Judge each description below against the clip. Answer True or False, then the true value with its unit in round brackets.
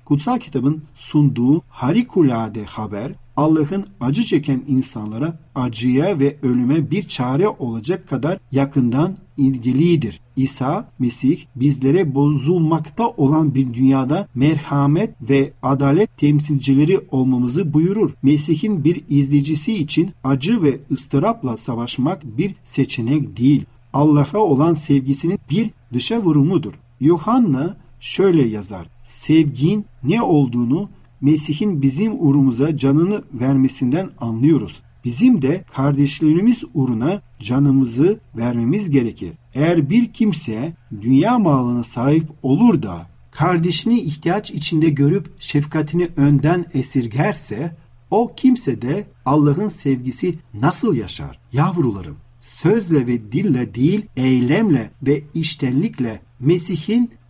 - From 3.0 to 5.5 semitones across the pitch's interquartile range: True (4.1 semitones)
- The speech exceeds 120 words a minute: False (105 wpm)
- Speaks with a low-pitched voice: False (145 Hz)